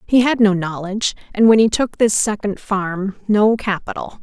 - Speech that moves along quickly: No, average, 185 wpm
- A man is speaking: No, female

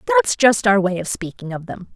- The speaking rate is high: Yes, fast, 245 wpm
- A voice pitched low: No, high, 215 Hz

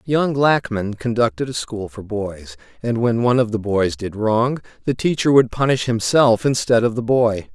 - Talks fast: No, average, 190 wpm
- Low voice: Yes, low, 115 Hz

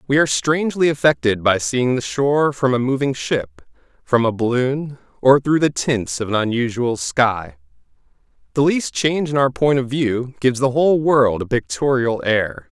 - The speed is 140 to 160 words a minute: No, average, 180 wpm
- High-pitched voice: No, low, 130 Hz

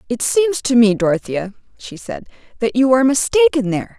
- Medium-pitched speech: No, very high, 250 Hz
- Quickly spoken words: No, average, 180 wpm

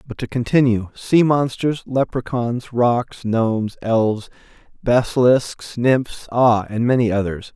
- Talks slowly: Yes, slow, 105 wpm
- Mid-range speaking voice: No, low, 120 Hz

